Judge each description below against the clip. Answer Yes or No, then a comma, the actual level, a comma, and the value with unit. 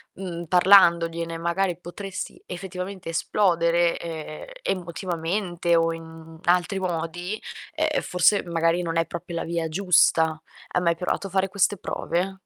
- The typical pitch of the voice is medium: Yes, medium, 175 Hz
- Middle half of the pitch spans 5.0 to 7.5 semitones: No, narrow, 2.1 semitones